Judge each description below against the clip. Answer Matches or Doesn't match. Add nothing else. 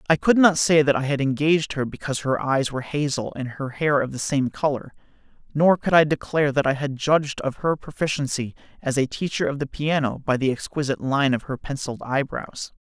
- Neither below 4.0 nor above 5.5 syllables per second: Doesn't match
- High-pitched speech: Doesn't match